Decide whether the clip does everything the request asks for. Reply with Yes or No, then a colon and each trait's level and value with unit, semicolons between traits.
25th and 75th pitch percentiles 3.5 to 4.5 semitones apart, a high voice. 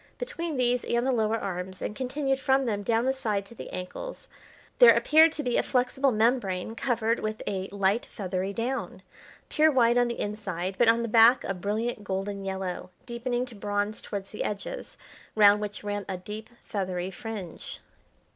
Yes: average, 3.8 semitones; high, 220 Hz